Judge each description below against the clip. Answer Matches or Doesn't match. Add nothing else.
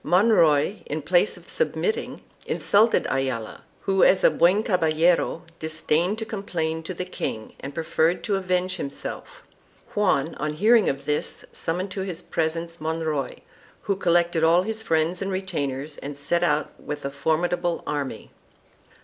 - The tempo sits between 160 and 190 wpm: Doesn't match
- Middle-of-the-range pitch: Matches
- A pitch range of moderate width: Matches